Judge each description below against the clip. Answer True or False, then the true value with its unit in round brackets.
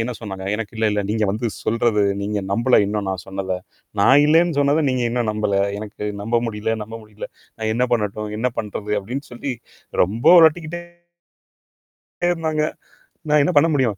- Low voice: True (115 Hz)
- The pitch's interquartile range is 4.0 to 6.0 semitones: True (4.5 semitones)